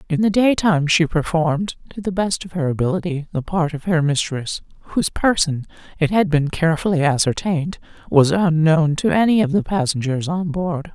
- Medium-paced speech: Yes, average, 170 wpm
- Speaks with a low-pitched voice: No, medium, 165 Hz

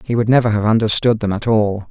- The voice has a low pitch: Yes, low, 110 Hz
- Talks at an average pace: No, fast, 250 wpm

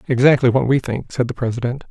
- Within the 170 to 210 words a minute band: No, fast, 220 wpm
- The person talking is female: No, male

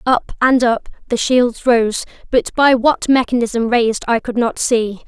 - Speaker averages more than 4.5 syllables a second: No, 4.2 syllables/s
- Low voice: No, high, 240 Hz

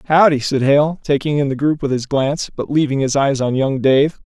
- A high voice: No, medium, 140 Hz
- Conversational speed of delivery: No, fast, 240 wpm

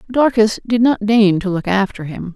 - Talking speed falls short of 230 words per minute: Yes, fast, 205 wpm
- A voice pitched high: Yes, high, 215 Hz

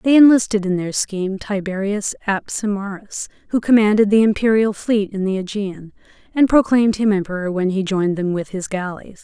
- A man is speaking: No, female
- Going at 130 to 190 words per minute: Yes, average, 170 wpm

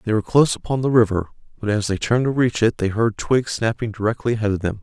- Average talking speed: No, fast, 260 wpm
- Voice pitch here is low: Yes, low, 110 Hz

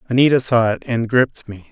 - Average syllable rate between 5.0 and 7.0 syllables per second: Yes, 5.6 syllables/s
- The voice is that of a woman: No, male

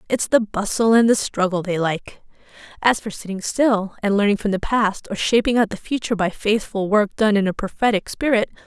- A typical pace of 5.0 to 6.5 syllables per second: Yes, 5.4 syllables/s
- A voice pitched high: Yes, high, 210 Hz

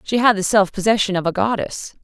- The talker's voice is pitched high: Yes, high, 200 Hz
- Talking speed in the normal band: No, fast, 235 wpm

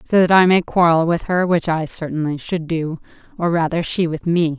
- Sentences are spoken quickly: Yes, fast, 210 wpm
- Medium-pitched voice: Yes, medium, 170 Hz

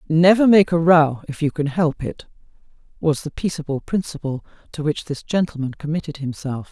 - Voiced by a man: No, female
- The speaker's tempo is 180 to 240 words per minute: No, average, 170 wpm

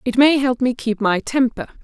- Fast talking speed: Yes, fast, 230 wpm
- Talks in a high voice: Yes, very high, 250 Hz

